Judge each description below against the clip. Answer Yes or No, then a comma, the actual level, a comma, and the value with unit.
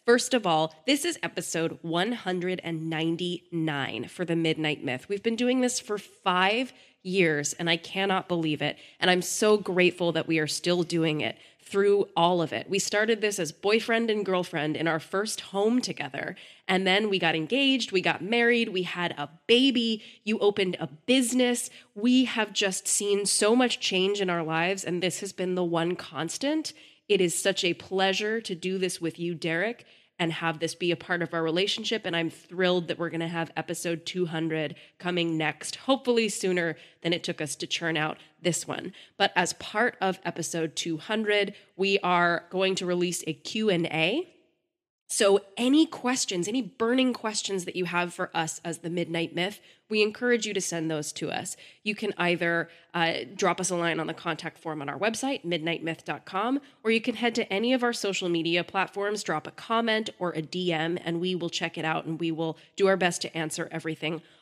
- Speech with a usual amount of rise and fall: Yes, average, 4.1 semitones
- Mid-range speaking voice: Yes, medium, 180 Hz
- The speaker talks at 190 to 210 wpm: Yes, average, 195 wpm